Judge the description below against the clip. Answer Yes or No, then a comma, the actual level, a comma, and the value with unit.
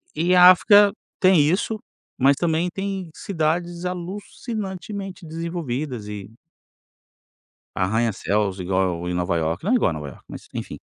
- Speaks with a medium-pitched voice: Yes, medium, 165 Hz